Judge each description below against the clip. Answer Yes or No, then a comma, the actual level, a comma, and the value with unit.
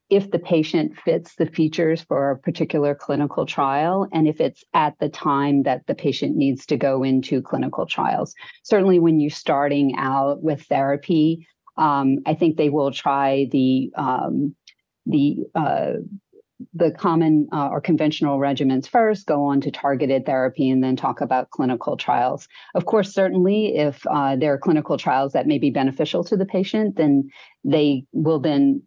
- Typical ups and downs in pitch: Yes, average, 3.7 semitones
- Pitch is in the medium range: Yes, medium, 150 Hz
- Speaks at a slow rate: No, average, 170 wpm